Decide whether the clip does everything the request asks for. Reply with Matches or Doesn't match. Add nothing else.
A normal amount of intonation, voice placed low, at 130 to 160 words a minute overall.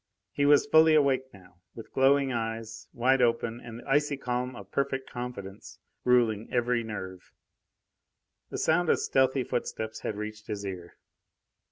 Matches